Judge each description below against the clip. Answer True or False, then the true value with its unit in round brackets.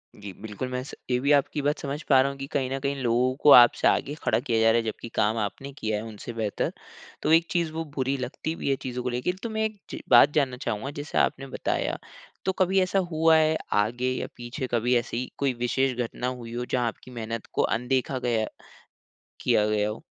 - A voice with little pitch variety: False (3.3 semitones)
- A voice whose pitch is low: True (125 Hz)